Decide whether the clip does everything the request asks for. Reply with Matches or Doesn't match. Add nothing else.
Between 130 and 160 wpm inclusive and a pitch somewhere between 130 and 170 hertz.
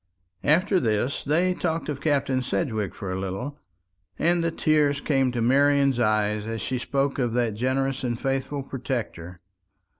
Matches